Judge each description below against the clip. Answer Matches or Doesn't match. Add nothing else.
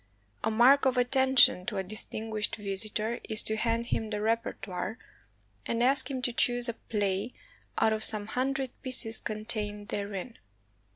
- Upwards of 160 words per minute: Doesn't match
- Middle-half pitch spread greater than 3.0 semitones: Doesn't match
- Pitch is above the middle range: Matches